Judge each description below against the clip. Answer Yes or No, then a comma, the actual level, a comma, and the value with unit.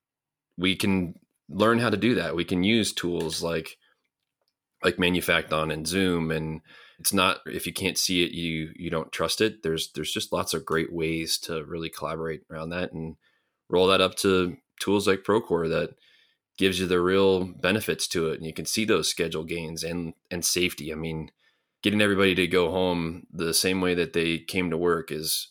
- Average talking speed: Yes, average, 195 wpm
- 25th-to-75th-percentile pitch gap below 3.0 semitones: Yes, narrow, 2.5 semitones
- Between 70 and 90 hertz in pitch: Yes, very low, 85 Hz